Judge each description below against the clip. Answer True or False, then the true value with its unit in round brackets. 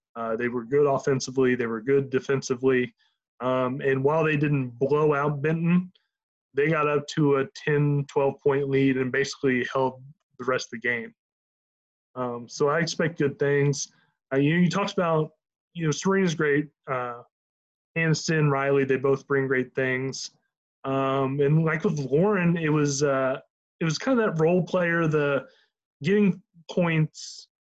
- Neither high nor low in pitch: True (145 Hz)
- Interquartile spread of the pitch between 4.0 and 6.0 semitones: False (3.1 semitones)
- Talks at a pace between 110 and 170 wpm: True (165 wpm)